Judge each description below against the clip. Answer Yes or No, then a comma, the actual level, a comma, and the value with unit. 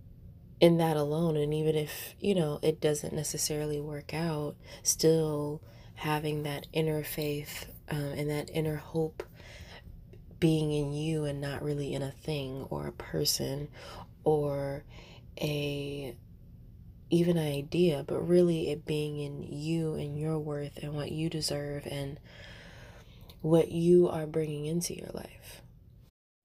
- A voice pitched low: No, medium, 150 Hz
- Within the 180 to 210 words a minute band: No, average, 140 wpm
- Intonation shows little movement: Yes, narrow, 1.9 semitones